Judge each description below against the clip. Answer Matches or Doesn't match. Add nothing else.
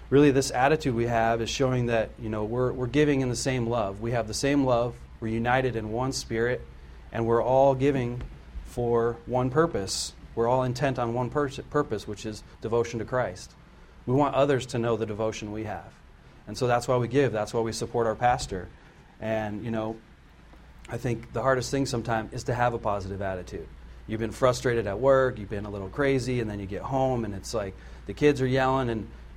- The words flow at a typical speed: Doesn't match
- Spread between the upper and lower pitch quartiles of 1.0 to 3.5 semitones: Matches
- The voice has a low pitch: Matches